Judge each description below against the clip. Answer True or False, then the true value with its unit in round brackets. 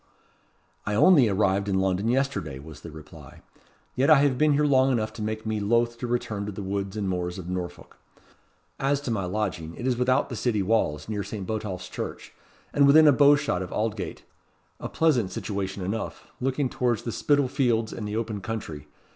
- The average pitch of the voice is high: False (110 Hz)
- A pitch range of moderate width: True (5.0 semitones)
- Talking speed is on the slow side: False (195 wpm)